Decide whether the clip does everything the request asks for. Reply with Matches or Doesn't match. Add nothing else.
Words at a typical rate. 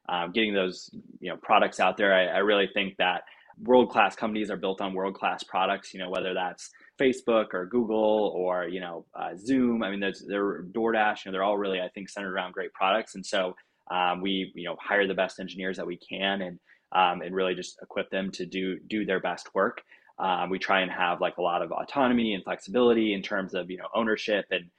Doesn't match